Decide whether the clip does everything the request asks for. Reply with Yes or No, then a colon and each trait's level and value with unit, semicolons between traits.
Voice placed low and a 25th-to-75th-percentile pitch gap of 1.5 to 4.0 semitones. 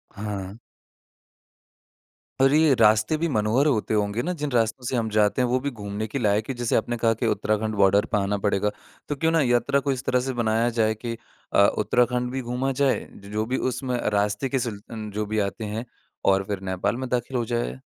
Yes: low, 115 Hz; average, 3.5 semitones